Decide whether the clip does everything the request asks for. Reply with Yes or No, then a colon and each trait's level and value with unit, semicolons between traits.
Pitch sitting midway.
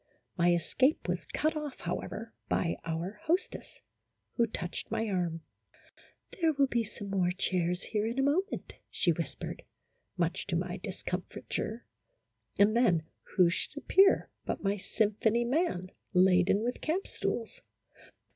No: high, 215 Hz